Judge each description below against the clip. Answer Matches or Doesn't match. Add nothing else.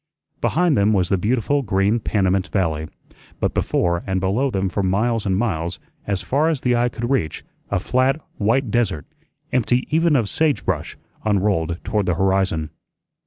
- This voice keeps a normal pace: Matches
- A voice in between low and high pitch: Doesn't match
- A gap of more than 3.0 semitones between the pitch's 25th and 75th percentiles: Matches